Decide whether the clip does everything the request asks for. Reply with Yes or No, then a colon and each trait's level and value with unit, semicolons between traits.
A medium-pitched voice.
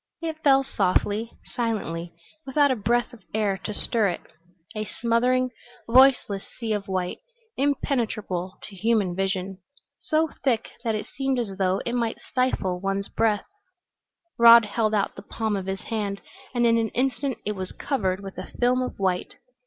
No: high, 220 Hz